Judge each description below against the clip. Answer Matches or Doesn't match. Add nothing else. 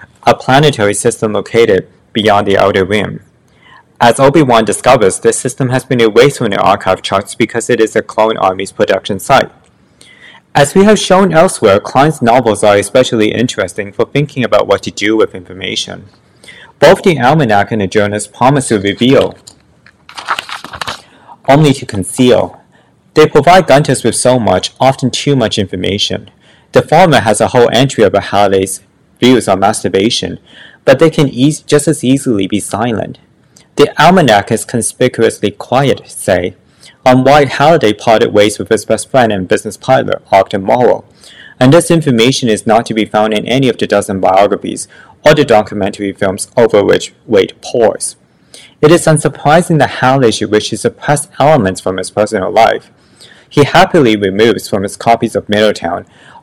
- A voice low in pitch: Matches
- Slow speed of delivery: Doesn't match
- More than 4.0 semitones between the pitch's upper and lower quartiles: Matches